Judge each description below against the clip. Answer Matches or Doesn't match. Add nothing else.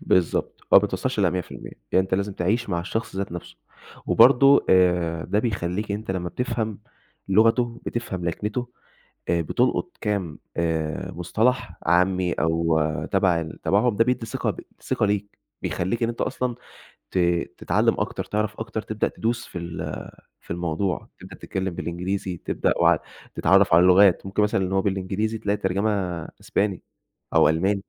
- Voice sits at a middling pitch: Doesn't match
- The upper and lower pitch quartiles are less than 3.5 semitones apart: Doesn't match